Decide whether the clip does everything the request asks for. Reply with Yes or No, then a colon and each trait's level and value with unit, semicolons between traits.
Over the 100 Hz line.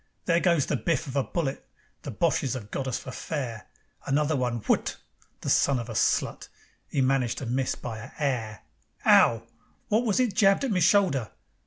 Yes: low, 135 Hz